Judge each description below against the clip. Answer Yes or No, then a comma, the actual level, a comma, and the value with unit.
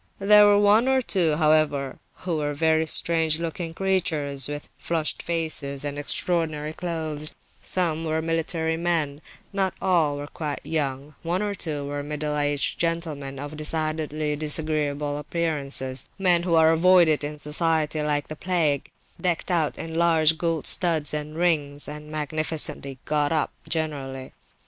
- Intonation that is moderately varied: No, narrow, 2.3 semitones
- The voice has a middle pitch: Yes, medium, 155 Hz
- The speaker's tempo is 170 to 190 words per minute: No, average, 145 wpm